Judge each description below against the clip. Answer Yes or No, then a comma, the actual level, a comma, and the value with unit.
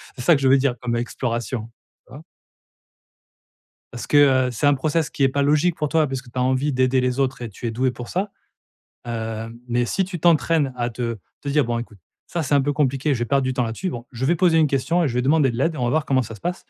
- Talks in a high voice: No, low, 130 Hz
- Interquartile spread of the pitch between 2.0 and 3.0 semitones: No, average, 3.6 semitones